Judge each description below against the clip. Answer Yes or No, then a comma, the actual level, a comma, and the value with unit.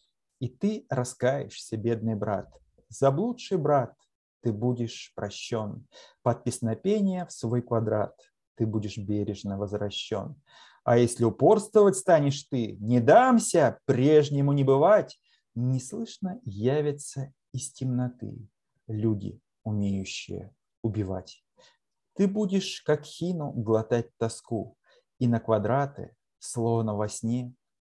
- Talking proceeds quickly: No, slow, 105 wpm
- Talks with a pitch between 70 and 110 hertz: No, low, 125 Hz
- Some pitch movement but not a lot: Yes, average, 4.9 semitones